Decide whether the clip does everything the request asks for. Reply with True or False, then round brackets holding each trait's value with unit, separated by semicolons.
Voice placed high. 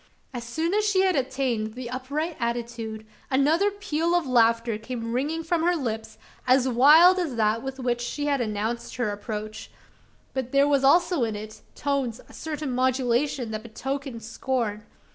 True (255 Hz)